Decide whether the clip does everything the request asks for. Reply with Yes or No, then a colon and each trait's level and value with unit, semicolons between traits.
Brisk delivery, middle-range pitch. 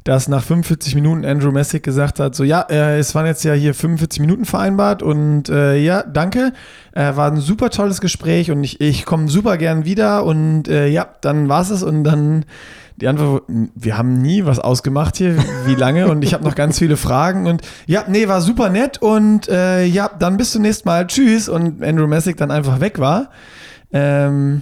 Yes: fast, 205 wpm; medium, 155 Hz